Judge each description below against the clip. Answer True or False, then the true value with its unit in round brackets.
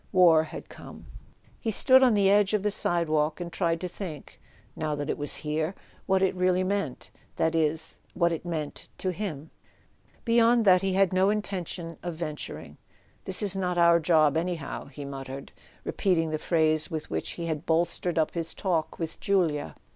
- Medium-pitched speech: True (170 Hz)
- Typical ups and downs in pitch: True (3.4 semitones)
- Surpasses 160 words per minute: True (175 wpm)